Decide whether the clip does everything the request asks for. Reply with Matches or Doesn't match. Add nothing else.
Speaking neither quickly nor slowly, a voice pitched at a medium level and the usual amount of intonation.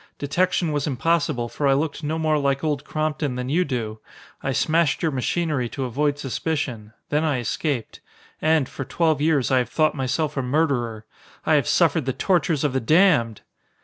Matches